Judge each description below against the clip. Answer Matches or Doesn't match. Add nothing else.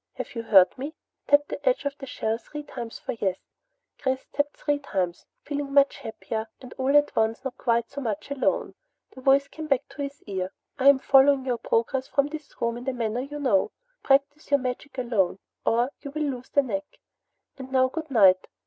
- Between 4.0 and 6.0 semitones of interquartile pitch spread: Doesn't match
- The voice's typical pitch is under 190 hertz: Doesn't match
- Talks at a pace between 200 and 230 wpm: Matches